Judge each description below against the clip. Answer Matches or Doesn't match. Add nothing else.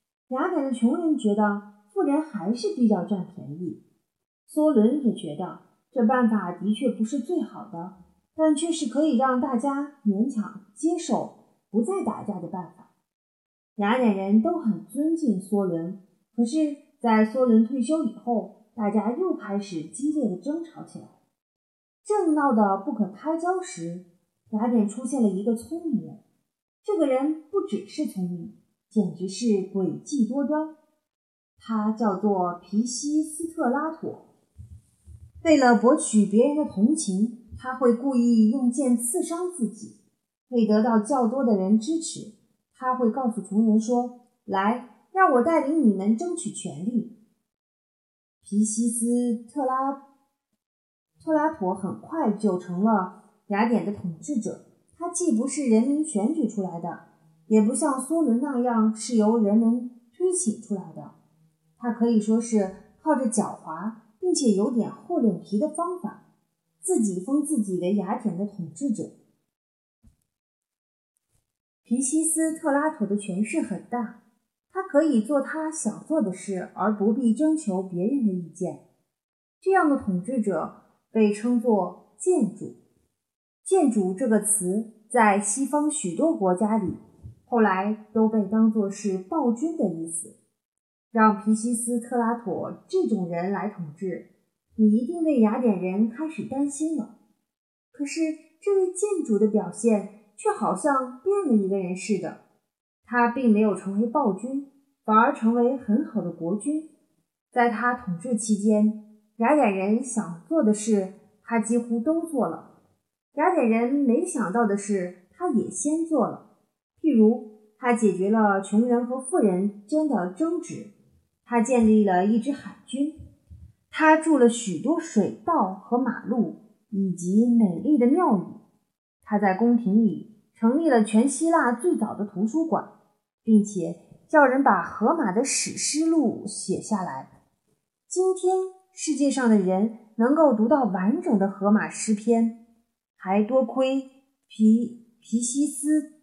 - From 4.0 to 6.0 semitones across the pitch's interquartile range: Matches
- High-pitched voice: Matches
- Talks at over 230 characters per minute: Doesn't match